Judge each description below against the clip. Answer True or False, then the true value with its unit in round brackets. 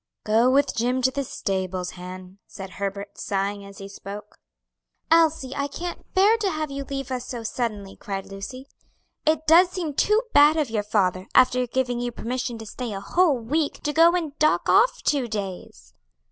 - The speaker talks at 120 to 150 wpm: False (185 wpm)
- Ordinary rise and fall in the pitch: False (6.8 semitones)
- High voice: True (245 Hz)